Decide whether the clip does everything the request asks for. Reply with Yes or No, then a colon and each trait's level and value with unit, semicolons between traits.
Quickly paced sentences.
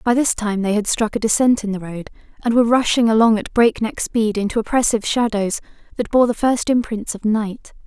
Yes: fast, 215 wpm